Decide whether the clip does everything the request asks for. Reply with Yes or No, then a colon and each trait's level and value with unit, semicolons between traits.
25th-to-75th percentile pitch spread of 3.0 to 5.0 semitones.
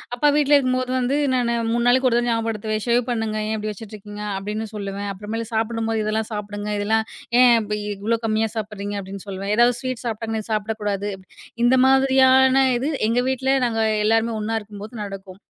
No: narrow, 2.6 semitones